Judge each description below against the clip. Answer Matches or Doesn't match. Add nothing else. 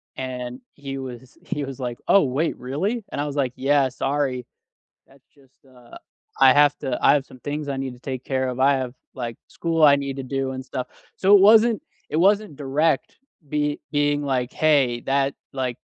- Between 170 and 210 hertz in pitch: Doesn't match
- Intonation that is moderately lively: Doesn't match